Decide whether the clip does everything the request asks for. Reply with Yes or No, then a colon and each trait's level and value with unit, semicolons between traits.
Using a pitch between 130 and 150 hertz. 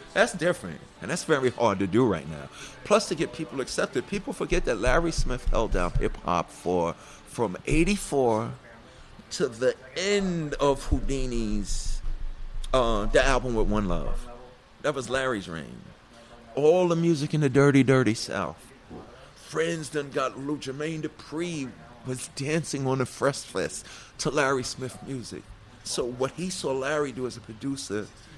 Yes: low, 135 Hz